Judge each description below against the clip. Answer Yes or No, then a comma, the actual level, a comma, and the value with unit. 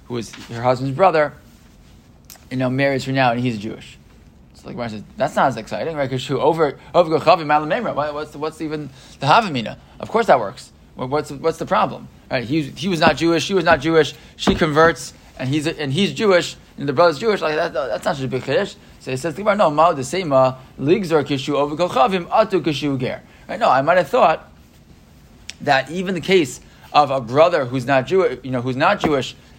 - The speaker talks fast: Yes, fast, 215 wpm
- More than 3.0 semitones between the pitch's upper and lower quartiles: Yes, average, 4.2 semitones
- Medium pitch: Yes, medium, 145 Hz